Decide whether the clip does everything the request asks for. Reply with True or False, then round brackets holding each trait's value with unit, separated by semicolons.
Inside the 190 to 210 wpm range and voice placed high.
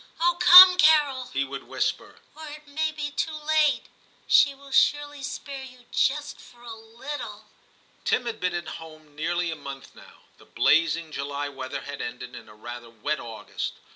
False (175 wpm; 240 Hz)